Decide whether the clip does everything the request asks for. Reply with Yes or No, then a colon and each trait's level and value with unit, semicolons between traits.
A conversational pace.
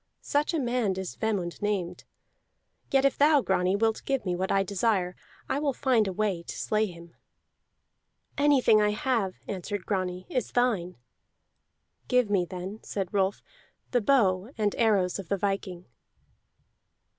Yes: average, 150 wpm